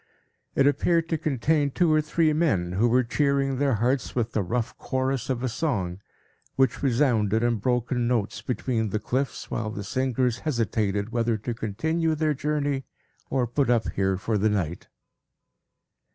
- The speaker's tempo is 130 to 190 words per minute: Yes, average, 165 wpm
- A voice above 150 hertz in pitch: No, low, 125 Hz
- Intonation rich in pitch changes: No, average, 4.2 semitones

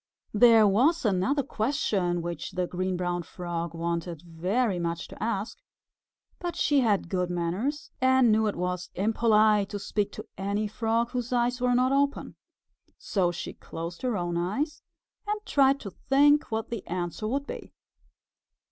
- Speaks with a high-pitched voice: Yes, high, 210 Hz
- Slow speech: No, average, 160 wpm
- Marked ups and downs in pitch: Yes, wide, 5.9 semitones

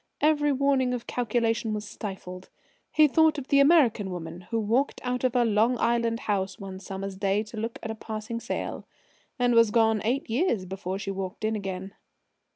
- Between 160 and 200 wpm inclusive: Yes, average, 185 wpm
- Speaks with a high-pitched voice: Yes, high, 225 Hz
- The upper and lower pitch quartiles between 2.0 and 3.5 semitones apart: No, average, 4.1 semitones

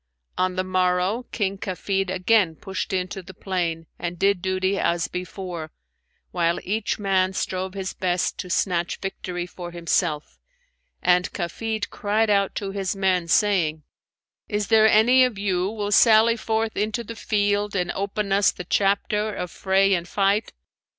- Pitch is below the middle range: No, high, 190 Hz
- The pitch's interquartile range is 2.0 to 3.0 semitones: Yes, narrow, 2.4 semitones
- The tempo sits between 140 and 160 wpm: Yes, average, 155 wpm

